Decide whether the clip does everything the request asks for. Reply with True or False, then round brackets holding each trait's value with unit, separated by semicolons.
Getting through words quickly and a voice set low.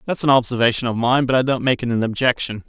True (270 wpm; 125 Hz)